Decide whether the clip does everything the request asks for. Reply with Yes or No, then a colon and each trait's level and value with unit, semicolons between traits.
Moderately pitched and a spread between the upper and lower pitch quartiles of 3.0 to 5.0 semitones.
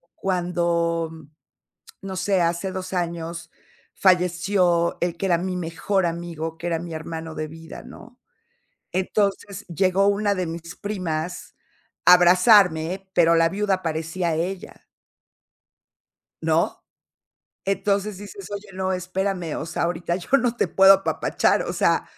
No: medium, 180 Hz; narrow, 2.4 semitones